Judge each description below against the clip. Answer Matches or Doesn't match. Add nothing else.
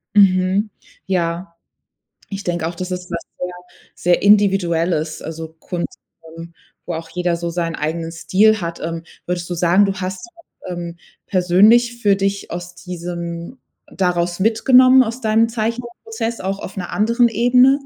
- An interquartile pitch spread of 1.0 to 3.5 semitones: Doesn't match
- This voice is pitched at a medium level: Matches